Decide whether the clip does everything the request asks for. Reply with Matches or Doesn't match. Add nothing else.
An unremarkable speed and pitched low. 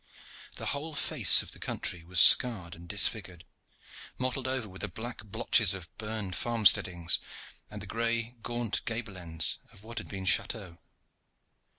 Matches